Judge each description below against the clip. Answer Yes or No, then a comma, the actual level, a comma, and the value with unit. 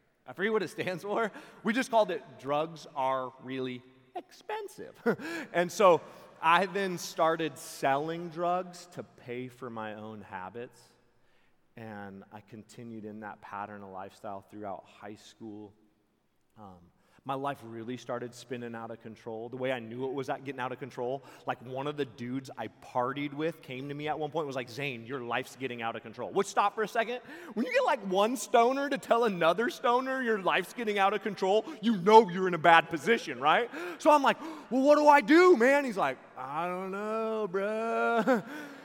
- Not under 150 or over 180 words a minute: No, average, 195 wpm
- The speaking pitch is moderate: Yes, medium, 150 Hz